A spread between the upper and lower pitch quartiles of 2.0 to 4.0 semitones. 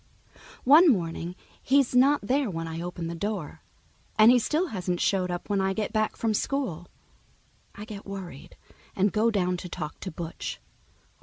No: average, 4.7 semitones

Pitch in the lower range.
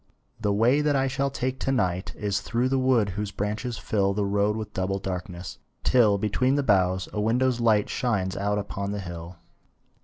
Yes: low, 105 Hz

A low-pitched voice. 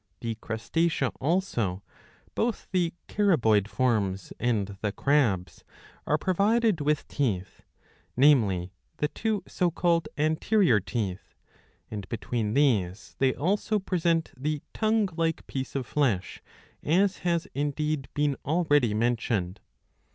No: medium, 145 Hz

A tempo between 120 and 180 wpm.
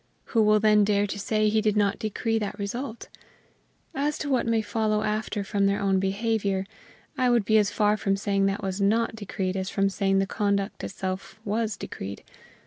No: average, 195 wpm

